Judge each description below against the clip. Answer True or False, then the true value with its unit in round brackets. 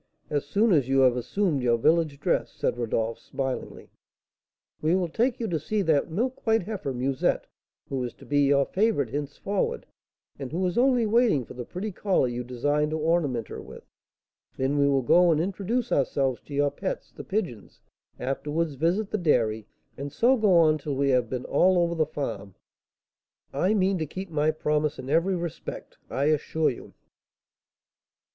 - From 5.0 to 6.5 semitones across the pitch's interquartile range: True (5.6 semitones)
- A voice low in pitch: False (150 Hz)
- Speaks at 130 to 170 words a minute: False (180 wpm)